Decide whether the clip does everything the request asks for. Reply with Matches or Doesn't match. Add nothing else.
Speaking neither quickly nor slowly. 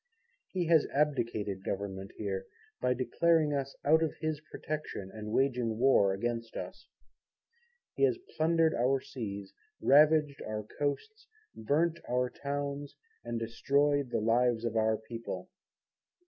Doesn't match